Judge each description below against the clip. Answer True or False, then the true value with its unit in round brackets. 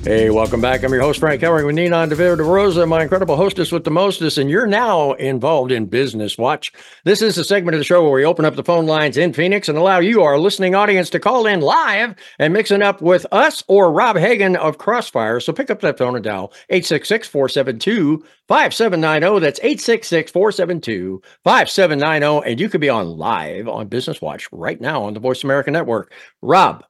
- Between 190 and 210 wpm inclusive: True (200 wpm)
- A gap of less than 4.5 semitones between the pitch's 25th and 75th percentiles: False (5.3 semitones)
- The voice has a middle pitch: True (160 Hz)